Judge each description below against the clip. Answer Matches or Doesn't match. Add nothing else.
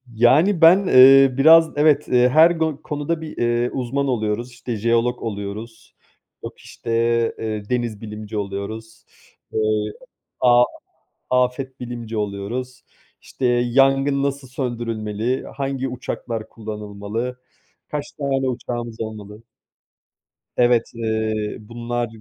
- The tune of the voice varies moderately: Matches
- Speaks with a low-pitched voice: Matches